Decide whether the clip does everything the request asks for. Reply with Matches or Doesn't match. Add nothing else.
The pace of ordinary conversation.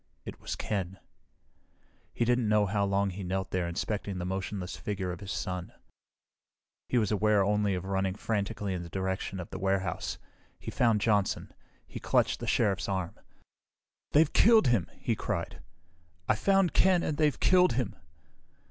Matches